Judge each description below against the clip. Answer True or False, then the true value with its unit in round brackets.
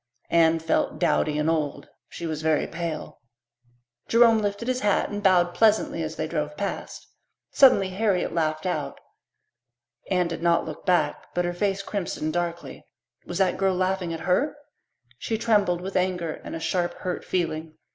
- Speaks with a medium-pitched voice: True (175 Hz)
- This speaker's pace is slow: False (165 wpm)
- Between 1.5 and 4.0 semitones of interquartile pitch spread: True (3.2 semitones)